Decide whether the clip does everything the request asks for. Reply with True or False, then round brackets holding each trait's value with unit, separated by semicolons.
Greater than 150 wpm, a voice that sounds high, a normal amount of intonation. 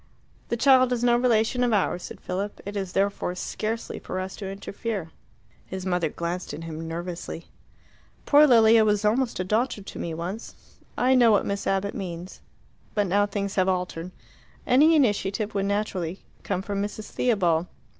True (170 wpm; 200 Hz; 3.7 semitones)